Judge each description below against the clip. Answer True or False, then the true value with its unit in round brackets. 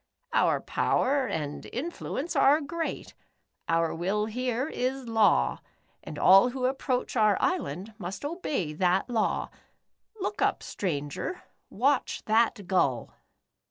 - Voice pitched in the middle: False (230 Hz)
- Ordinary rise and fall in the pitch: False (6.4 semitones)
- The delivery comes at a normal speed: False (125 wpm)